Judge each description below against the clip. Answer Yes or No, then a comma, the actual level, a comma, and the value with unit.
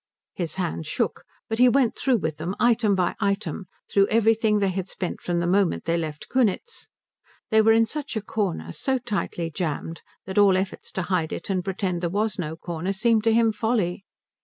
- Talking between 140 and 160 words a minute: No, average, 200 wpm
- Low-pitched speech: No, high, 195 Hz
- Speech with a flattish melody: No, average, 4.2 semitones